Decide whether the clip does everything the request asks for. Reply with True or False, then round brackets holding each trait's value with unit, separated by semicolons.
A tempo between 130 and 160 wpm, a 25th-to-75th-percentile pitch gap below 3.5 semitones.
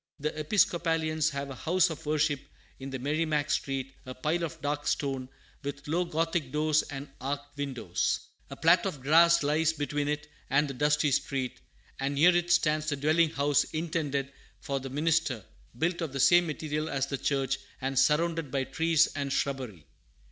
False (170 wpm; 2.8 semitones)